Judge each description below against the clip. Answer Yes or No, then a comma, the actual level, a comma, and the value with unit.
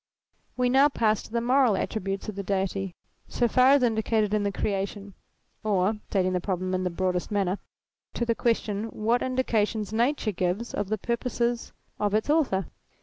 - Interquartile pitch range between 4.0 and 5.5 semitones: No, average, 3.4 semitones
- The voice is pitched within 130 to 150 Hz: No, high, 215 Hz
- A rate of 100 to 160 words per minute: No, average, 175 wpm